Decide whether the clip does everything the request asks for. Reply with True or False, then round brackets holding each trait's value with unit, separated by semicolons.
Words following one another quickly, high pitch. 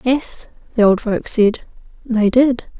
False (150 wpm; 230 Hz)